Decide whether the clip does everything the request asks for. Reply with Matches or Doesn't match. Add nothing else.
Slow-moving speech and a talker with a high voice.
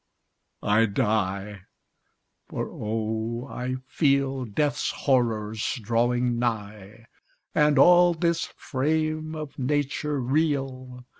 Doesn't match